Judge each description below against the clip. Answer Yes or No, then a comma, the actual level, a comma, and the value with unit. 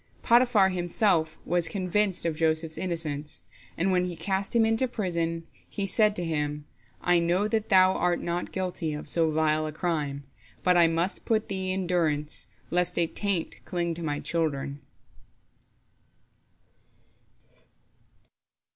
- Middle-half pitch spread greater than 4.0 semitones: No, average, 3.0 semitones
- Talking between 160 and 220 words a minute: No, average, 145 wpm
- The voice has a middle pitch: Yes, medium, 175 Hz